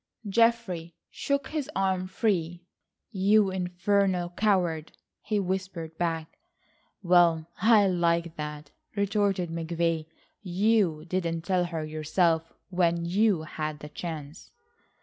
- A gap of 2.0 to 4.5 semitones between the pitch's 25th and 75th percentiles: Yes, average, 3.1 semitones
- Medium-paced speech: No, slow, 110 wpm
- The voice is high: No, medium, 175 Hz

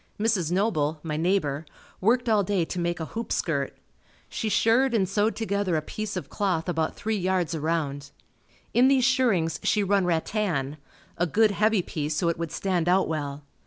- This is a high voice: No, medium, 180 Hz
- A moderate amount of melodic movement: Yes, average, 4.8 semitones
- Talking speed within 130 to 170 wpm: No, average, 180 wpm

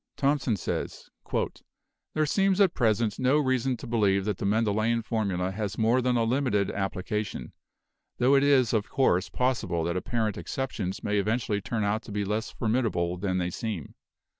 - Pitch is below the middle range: Yes, low, 110 Hz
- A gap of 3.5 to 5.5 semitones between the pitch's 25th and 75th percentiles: Yes, average, 4.2 semitones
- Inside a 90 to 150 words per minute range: No, average, 165 wpm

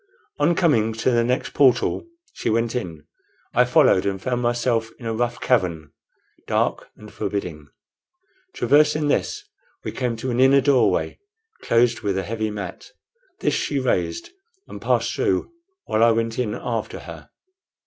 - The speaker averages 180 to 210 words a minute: No, average, 155 wpm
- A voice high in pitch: No, low, 115 Hz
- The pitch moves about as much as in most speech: Yes, average, 3.3 semitones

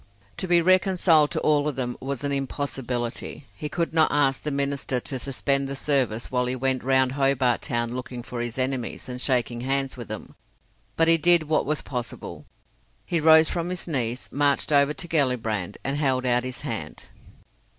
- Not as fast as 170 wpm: No, average, 185 wpm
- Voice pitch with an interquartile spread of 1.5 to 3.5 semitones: Yes, average, 3.2 semitones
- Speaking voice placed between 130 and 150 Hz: Yes, low, 135 Hz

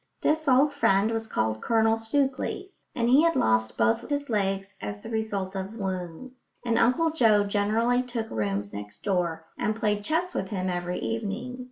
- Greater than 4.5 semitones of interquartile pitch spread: Yes, average, 5.1 semitones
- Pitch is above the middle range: Yes, high, 215 Hz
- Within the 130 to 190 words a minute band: Yes, average, 175 wpm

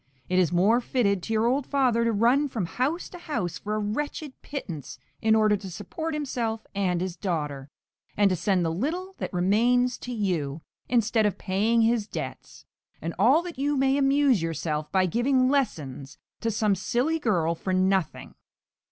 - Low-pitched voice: No, high, 220 Hz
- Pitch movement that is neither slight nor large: No, wide, 5.8 semitones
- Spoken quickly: No, average, 180 wpm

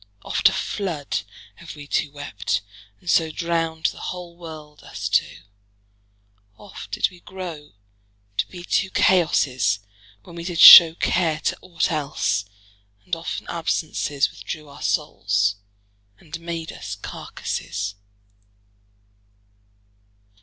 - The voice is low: No, medium, 160 Hz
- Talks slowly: Yes, slow, 120 wpm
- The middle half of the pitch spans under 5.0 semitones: Yes, average, 3.1 semitones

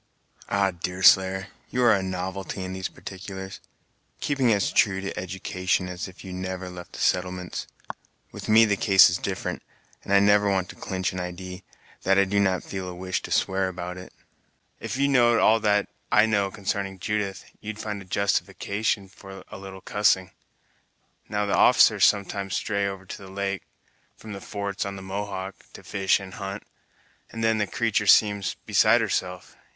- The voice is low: Yes, very low, 95 Hz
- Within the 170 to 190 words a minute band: Yes, average, 180 wpm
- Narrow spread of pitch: Yes, narrow, 1.5 semitones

